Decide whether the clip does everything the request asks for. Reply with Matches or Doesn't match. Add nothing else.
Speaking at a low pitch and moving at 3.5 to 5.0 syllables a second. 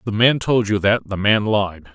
Matches